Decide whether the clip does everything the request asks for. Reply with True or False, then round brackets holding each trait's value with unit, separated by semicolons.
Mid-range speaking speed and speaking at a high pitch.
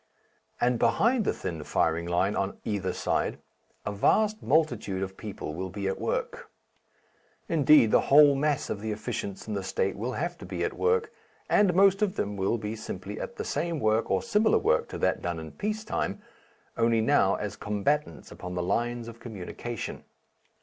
False (185 wpm; 115 Hz)